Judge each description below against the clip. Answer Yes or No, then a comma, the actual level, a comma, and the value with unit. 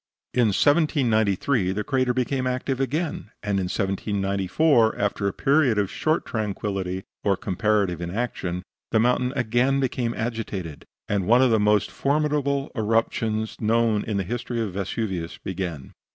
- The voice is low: Yes, low, 110 Hz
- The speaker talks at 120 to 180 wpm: Yes, average, 140 wpm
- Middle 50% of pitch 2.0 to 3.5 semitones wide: No, average, 4.5 semitones